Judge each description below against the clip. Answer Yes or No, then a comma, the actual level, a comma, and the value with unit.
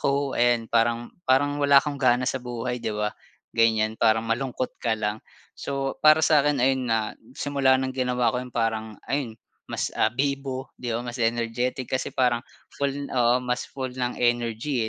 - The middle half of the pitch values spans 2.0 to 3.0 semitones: Yes, average, 2.7 semitones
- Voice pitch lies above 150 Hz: No, low, 125 Hz